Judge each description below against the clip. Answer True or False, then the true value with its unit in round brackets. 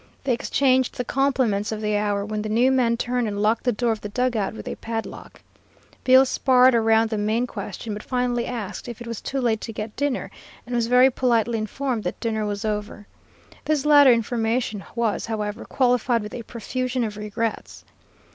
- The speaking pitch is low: False (230 Hz)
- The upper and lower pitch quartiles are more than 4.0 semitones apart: False (2.7 semitones)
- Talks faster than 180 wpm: True (195 wpm)